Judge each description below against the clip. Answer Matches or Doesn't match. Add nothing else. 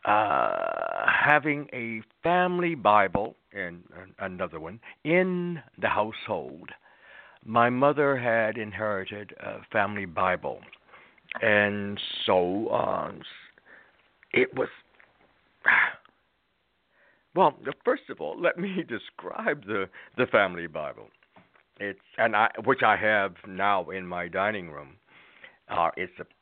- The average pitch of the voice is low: Matches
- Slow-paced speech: Matches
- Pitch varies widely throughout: Matches